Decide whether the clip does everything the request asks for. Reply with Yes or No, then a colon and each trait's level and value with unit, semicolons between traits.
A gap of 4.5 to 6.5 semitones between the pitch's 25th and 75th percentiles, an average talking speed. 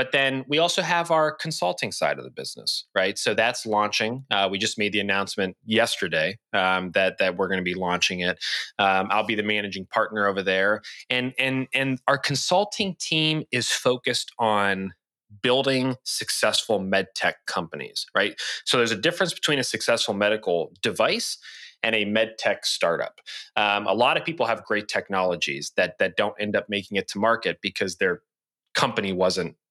Yes: average, 5.1 semitones; average, 180 wpm